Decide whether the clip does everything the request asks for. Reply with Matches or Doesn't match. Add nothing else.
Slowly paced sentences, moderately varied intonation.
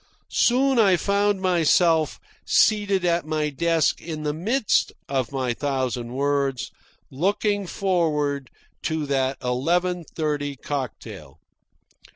Matches